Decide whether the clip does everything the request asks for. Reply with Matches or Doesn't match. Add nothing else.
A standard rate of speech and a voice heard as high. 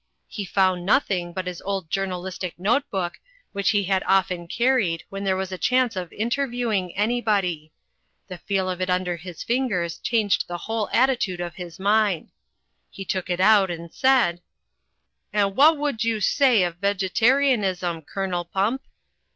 Matches